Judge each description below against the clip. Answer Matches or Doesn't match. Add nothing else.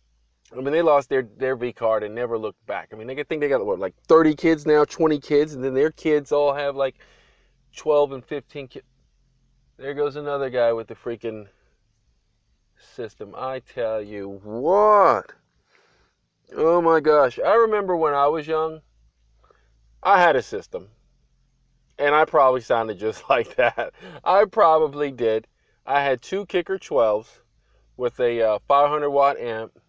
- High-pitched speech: Doesn't match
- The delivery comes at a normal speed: Matches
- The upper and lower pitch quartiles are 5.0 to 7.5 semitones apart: Matches